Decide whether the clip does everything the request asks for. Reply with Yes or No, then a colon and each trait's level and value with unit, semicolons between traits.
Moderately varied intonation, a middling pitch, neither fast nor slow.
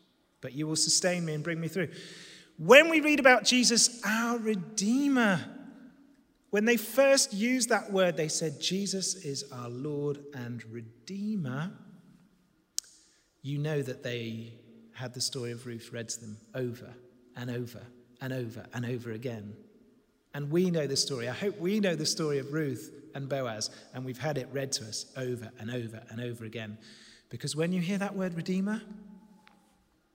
No: wide, 8.3 semitones; medium, 155 Hz; average, 170 wpm